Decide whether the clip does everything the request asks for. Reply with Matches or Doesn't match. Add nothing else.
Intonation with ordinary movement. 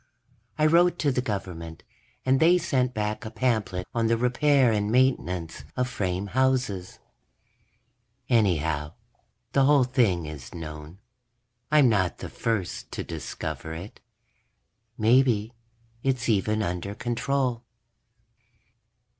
Doesn't match